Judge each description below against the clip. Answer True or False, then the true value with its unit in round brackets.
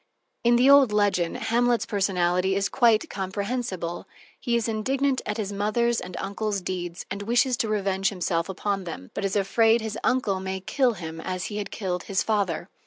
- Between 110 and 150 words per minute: False (185 wpm)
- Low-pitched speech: False (200 Hz)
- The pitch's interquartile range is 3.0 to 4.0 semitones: True (3.5 semitones)